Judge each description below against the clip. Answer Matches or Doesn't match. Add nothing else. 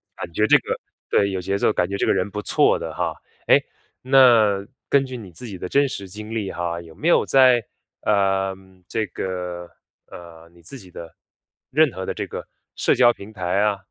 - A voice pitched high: Doesn't match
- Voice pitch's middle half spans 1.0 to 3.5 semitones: Doesn't match